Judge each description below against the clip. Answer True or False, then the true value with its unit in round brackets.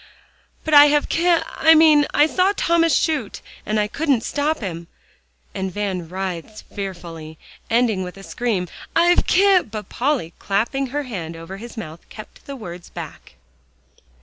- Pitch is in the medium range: False (225 Hz)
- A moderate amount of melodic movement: False (8.1 semitones)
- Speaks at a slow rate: False (155 wpm)